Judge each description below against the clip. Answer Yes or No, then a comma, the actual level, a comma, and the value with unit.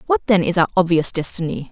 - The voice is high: No, medium, 180 Hz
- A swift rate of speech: Yes, fast, 210 wpm